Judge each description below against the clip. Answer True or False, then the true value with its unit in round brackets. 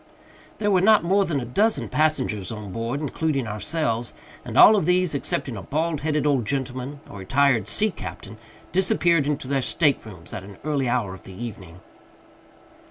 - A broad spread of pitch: True (6.2 semitones)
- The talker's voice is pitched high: False (140 Hz)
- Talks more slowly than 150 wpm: False (170 wpm)